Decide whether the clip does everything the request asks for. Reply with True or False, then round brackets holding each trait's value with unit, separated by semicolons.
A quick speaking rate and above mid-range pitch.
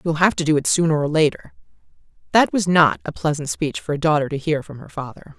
False (245 wpm; 155 Hz)